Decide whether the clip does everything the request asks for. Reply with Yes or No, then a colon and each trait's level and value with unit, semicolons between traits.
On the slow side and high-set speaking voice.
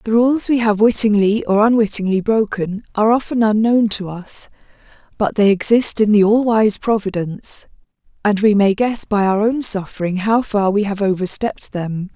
No: average, 175 wpm; high, 210 Hz